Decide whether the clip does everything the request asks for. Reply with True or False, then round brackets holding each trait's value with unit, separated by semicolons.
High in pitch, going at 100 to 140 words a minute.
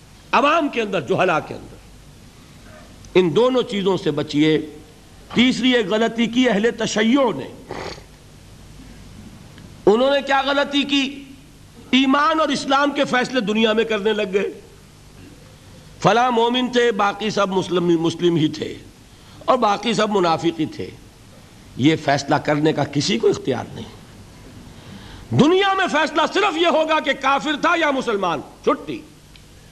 True (215 Hz; 135 wpm)